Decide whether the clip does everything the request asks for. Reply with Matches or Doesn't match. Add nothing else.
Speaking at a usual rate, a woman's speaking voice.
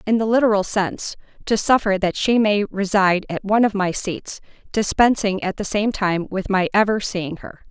Matches